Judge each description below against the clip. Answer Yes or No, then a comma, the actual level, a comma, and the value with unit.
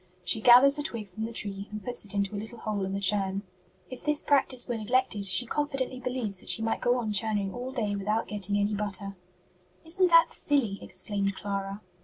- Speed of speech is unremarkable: No, fast, 210 wpm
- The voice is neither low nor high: No, high, 215 Hz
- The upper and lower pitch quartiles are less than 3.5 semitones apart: No, average, 3.9 semitones